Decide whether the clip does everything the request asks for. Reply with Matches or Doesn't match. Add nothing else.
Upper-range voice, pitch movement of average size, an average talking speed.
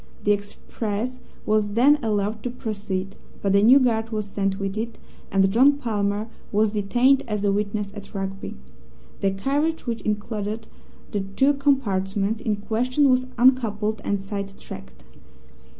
Matches